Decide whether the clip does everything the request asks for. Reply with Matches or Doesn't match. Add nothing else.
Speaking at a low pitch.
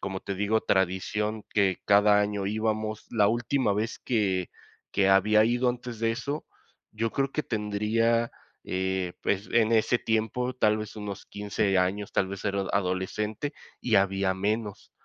Matches